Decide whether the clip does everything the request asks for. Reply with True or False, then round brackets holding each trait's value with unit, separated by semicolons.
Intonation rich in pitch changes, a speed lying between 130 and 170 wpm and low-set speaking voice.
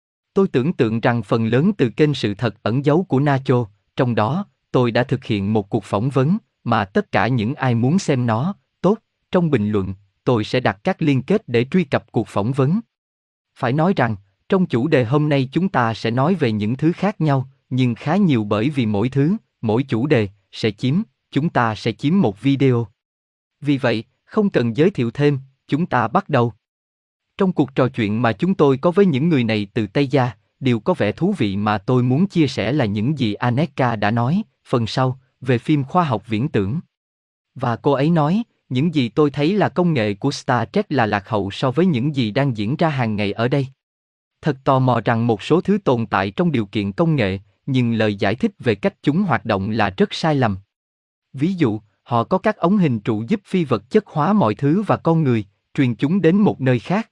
False (5.9 semitones; 225 wpm; 130 Hz)